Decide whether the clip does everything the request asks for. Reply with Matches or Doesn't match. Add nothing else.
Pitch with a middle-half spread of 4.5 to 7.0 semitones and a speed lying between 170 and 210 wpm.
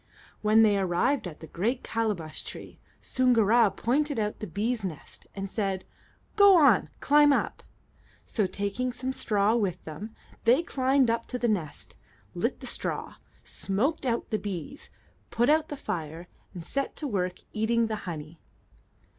Doesn't match